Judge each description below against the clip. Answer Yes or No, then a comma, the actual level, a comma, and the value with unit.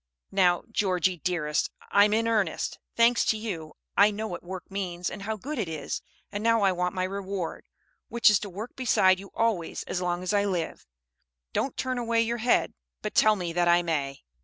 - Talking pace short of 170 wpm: No, average, 200 wpm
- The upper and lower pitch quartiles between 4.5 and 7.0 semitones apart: No, average, 3.7 semitones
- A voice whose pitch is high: Yes, high, 195 Hz